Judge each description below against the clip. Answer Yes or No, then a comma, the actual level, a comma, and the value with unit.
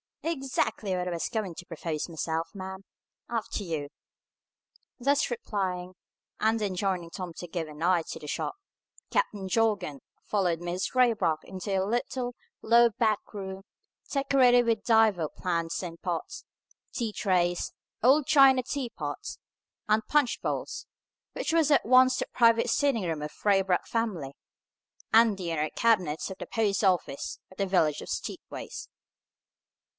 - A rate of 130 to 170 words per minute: Yes, average, 150 wpm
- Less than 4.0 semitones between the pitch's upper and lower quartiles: No, average, 5.0 semitones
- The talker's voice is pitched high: Yes, high, 195 Hz